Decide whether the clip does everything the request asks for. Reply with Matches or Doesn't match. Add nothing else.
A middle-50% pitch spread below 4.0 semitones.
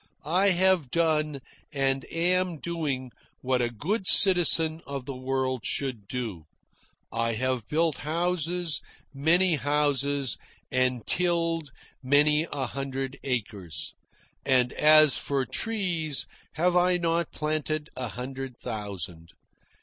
Doesn't match